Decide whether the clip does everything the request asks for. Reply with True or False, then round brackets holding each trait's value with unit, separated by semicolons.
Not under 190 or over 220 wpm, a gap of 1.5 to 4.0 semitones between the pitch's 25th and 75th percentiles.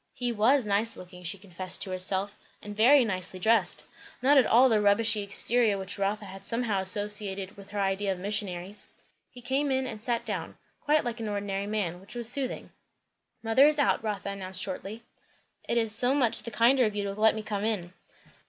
True (195 wpm; 3.2 semitones)